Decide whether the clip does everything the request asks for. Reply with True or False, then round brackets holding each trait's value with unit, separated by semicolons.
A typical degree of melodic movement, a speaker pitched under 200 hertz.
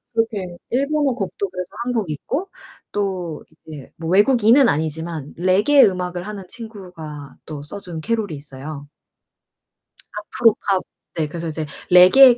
False (5.9 semitones; 185 Hz)